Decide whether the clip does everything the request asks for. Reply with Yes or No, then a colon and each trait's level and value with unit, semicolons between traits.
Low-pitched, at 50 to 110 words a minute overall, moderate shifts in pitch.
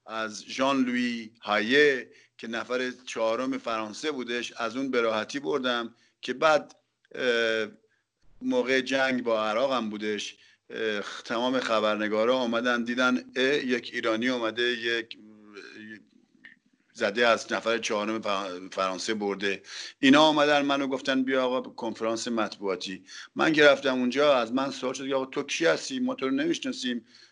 No: low, 120 Hz; average, 130 wpm; average, 3.2 semitones